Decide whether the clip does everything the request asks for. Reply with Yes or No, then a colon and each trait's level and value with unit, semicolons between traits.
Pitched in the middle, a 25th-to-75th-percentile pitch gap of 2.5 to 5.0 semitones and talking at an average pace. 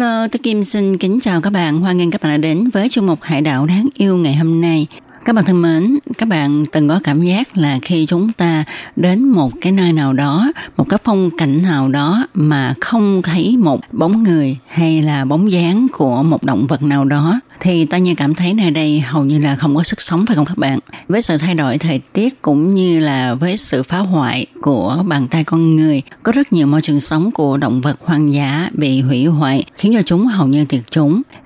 Yes: medium, 165 Hz; average, 4.7 semitones; average, 235 wpm